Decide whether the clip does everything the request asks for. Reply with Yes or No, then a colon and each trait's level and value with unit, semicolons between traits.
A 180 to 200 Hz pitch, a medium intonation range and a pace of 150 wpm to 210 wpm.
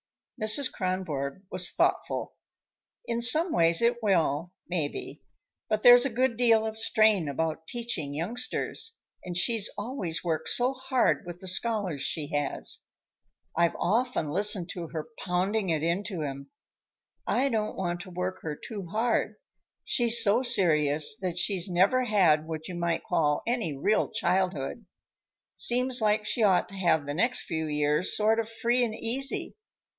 No: high, 190 Hz; wide, 5.7 semitones; average, 155 wpm